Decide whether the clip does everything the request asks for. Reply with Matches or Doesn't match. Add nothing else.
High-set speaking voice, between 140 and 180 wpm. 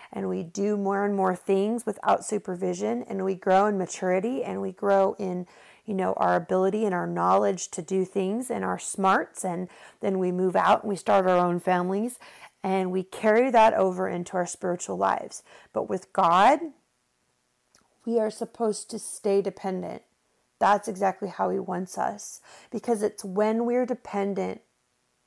Matches